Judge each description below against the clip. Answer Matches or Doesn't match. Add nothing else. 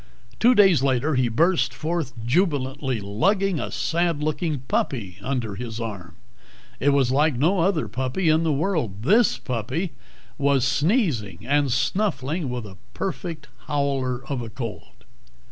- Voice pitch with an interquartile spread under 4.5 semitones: Doesn't match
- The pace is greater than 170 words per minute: Doesn't match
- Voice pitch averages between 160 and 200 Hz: Doesn't match